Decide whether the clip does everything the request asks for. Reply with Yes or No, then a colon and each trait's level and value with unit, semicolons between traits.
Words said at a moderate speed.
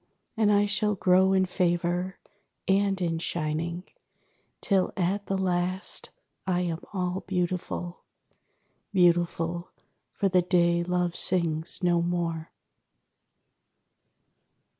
No: slow, 100 wpm